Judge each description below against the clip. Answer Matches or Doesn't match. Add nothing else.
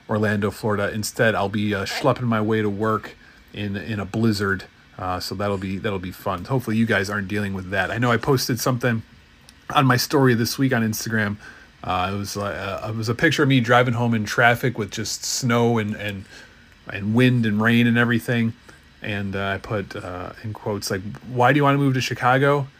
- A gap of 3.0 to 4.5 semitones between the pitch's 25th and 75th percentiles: Matches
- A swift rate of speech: Matches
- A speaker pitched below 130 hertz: Matches